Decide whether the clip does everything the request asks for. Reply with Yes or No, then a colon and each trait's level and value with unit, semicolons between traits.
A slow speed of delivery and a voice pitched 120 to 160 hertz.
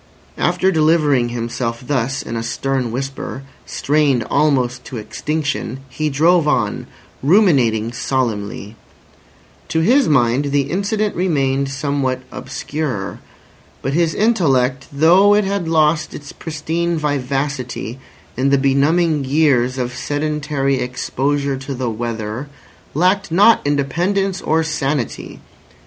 Yes: slow, 115 wpm; medium, 140 Hz